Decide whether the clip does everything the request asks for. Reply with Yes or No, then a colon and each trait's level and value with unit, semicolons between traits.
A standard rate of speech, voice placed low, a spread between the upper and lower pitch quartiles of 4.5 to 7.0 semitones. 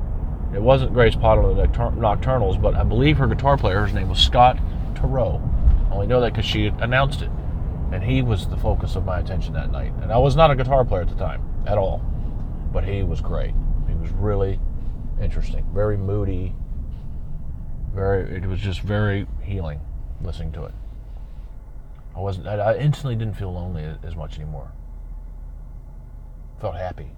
Yes: average, 175 wpm; very low, 90 Hz; wide, 5.4 semitones